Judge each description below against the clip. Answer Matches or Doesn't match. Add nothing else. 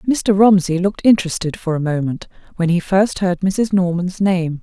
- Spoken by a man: Doesn't match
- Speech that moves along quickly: Doesn't match